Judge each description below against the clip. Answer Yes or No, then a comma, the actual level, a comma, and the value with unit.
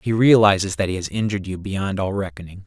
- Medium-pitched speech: No, low, 100 Hz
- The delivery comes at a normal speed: No, fast, 225 wpm